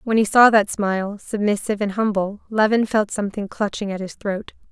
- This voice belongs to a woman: Yes, female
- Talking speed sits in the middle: Yes, average, 190 wpm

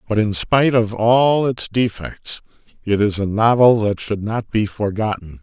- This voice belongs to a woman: No, male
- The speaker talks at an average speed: Yes, average, 175 wpm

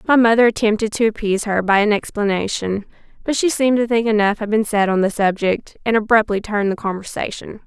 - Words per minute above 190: Yes, fast, 205 wpm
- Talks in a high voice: Yes, high, 215 Hz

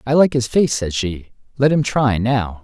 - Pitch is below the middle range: Yes, low, 125 Hz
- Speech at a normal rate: No, fast, 225 wpm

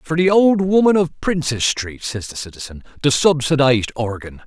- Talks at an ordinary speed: Yes, average, 175 wpm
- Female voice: No, male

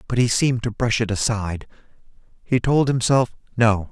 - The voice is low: Yes, low, 115 Hz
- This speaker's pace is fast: No, average, 170 wpm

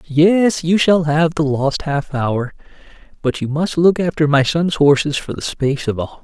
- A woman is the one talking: No, male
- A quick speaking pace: Yes, fast, 220 wpm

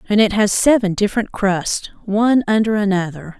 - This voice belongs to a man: No, female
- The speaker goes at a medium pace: Yes, average, 160 wpm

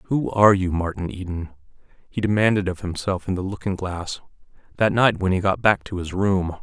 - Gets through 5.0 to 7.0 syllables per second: Yes, 5.4 syllables/s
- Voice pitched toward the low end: Yes, very low, 95 Hz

